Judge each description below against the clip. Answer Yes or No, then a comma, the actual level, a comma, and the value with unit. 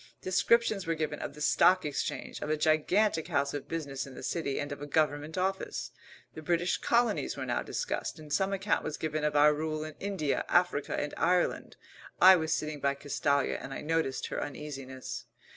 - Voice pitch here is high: No, medium, 155 Hz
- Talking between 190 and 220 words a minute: Yes, average, 195 wpm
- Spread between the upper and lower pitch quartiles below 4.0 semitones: Yes, average, 3.5 semitones